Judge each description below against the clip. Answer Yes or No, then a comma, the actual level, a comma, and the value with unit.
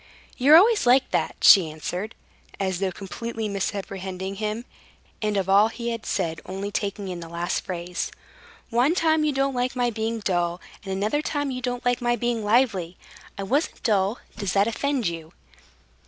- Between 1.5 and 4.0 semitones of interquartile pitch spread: No, average, 4.5 semitones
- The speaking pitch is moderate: No, high, 210 Hz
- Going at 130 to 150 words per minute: No, average, 175 wpm